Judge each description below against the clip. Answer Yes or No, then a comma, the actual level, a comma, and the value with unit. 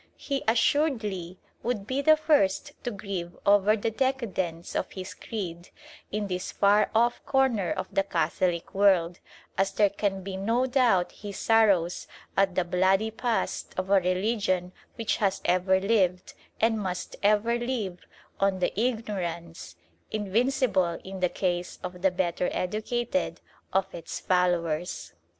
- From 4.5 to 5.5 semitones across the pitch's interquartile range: No, average, 3.7 semitones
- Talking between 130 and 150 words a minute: Yes, average, 140 wpm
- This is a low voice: No, high, 195 Hz